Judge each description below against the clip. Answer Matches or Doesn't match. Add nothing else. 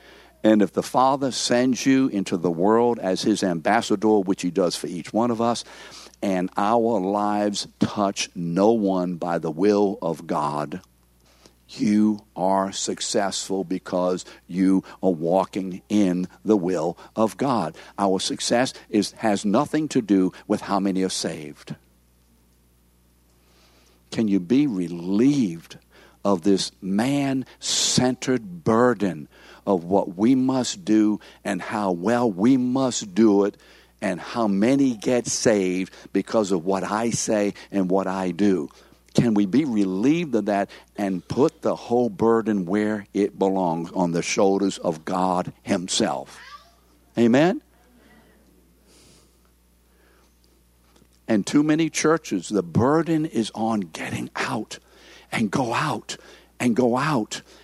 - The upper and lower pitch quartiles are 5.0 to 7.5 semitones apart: Doesn't match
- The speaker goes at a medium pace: Doesn't match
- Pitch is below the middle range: Matches